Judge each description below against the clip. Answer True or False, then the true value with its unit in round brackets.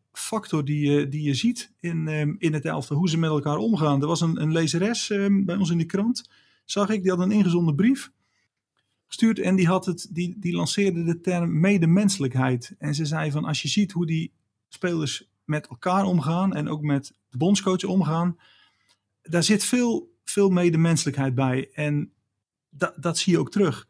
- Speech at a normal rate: True (185 wpm)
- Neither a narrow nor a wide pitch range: True (4.5 semitones)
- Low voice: False (170 Hz)